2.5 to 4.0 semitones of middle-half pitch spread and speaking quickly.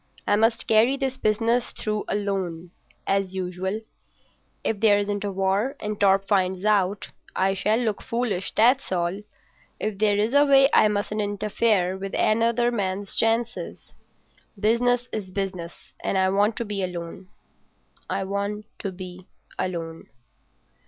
No: average, 2.8 semitones; average, 140 wpm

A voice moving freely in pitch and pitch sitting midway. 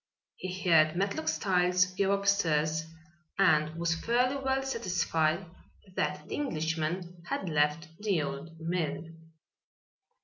No: average, 3.7 semitones; medium, 175 Hz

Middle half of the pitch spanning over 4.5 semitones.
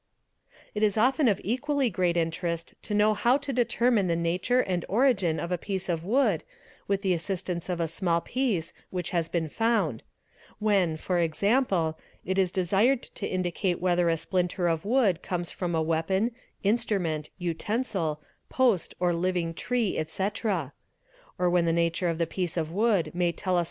No: average, 4.1 semitones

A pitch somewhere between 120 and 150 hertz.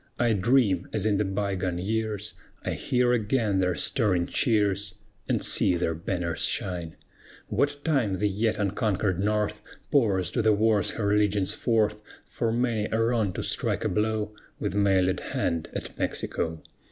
No: low, 105 Hz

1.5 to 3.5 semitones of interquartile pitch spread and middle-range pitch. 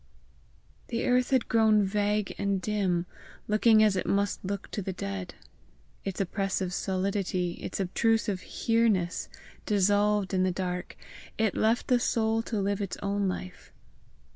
No: narrow, 2.6 semitones; high, 200 Hz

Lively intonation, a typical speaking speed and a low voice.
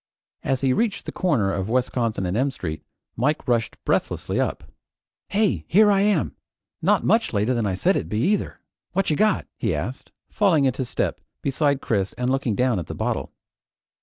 Yes: wide, 7.3 semitones; average, 185 wpm; low, 130 Hz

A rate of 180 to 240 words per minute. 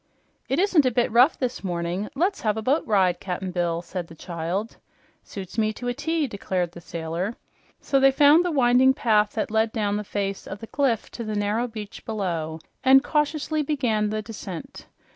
Yes: average, 195 wpm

